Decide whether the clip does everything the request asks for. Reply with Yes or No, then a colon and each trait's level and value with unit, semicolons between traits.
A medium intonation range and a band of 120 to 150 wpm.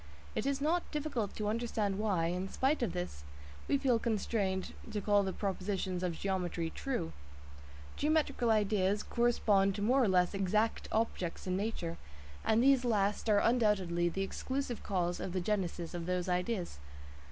No: average, 4.2 semitones; average, 160 wpm